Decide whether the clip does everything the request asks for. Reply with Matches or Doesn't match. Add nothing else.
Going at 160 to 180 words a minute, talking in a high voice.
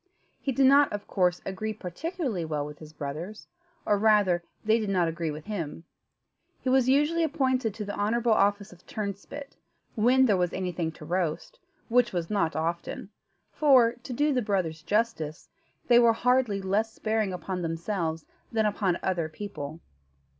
Matches